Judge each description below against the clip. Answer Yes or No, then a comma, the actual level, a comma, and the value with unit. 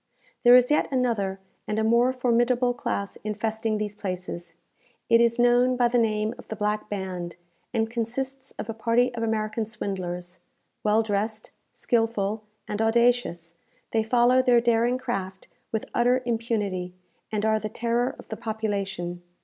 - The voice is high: Yes, high, 225 Hz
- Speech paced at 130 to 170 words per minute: Yes, average, 155 wpm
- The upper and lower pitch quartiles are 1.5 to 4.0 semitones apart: Yes, narrow, 2.6 semitones